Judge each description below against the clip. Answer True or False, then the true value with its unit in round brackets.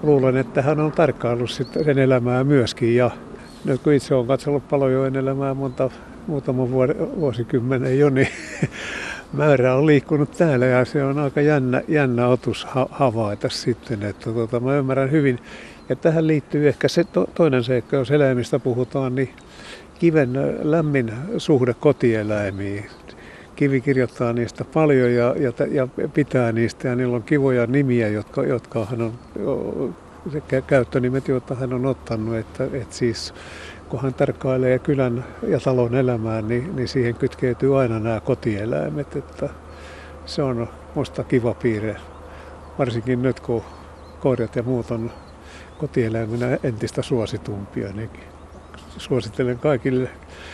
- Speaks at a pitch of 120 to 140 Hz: True (130 Hz)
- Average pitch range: True (3.0 semitones)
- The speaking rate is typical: True (130 wpm)